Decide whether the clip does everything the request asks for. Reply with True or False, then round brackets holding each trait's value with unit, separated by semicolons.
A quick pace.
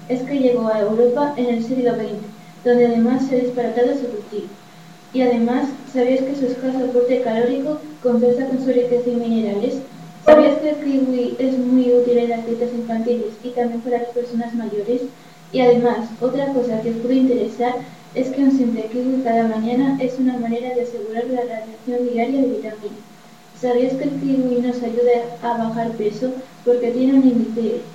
False (180 wpm)